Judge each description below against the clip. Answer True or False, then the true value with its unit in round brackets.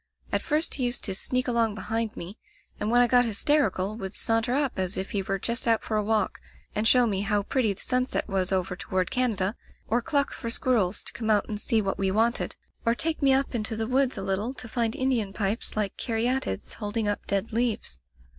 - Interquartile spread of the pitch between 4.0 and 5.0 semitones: False (3.6 semitones)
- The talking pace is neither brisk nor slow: False (225 wpm)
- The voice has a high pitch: True (225 Hz)